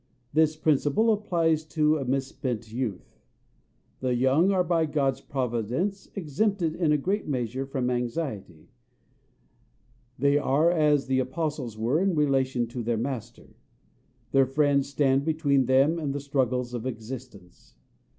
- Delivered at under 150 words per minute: Yes, slow, 135 wpm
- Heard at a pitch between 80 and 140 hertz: Yes, low, 135 Hz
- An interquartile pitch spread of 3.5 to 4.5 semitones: Yes, average, 3.8 semitones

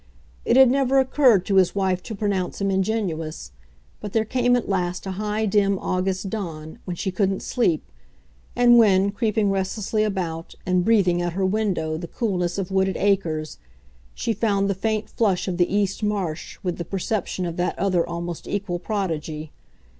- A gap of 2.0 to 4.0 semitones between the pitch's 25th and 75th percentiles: Yes, average, 3.2 semitones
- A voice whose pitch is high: Yes, high, 195 Hz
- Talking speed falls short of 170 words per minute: No, average, 175 wpm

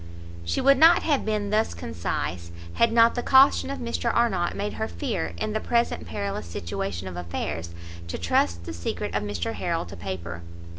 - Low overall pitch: Yes, very low, 95 Hz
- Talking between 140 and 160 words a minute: No, average, 185 wpm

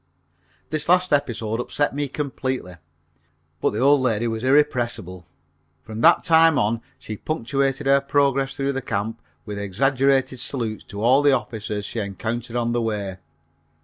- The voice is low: Yes, low, 125 Hz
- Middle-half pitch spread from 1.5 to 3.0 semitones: No, average, 4.0 semitones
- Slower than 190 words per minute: Yes, average, 150 wpm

